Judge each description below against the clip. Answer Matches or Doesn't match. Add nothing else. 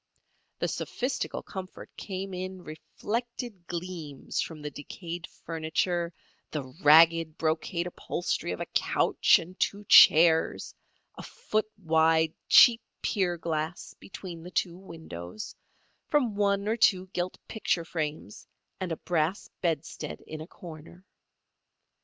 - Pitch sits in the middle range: Matches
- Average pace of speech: Doesn't match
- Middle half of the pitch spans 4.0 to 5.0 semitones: Doesn't match